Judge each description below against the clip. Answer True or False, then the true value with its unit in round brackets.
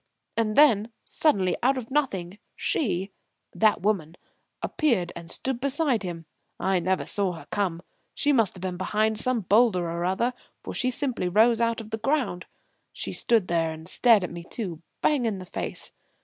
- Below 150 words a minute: False (175 wpm)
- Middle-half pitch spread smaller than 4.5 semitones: False (5.2 semitones)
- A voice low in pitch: False (210 Hz)